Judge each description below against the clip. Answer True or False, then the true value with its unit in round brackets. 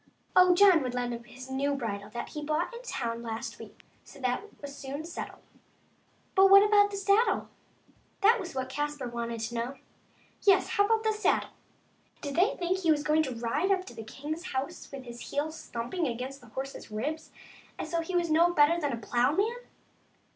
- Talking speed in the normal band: False (210 wpm)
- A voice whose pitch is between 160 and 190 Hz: False (295 Hz)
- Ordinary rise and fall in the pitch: False (6.8 semitones)